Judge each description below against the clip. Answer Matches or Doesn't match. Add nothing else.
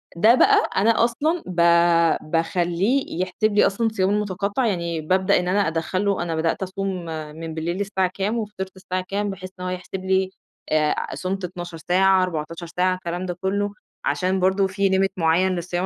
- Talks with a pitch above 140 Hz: Matches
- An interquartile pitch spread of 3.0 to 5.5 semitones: Doesn't match